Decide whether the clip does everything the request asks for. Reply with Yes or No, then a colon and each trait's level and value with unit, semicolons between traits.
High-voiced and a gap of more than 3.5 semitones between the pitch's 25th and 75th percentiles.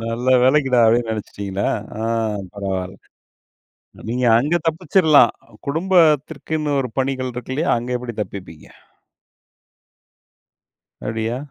No: low, 125 Hz; average, 4.9 semitones